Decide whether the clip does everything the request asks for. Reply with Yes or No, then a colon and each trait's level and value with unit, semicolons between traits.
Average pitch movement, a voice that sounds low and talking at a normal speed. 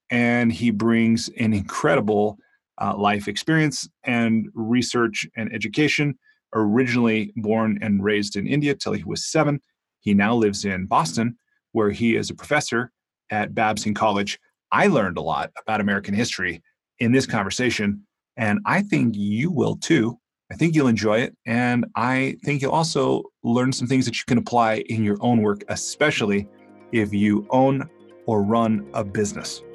Yes: average, 3.5 semitones; low, 115 Hz; average, 160 wpm